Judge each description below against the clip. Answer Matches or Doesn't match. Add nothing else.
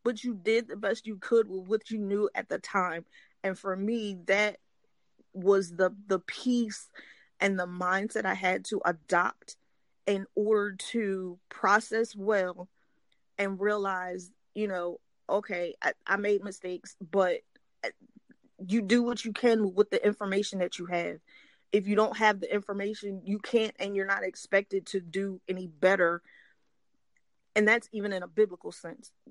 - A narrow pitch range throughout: Matches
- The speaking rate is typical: Matches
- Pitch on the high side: Matches